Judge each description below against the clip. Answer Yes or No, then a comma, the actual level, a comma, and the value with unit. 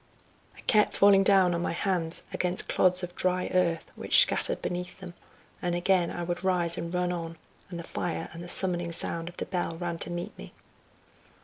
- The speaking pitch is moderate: Yes, medium, 175 Hz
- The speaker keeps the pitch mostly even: Yes, narrow, 1.3 semitones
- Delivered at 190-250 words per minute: Yes, average, 200 wpm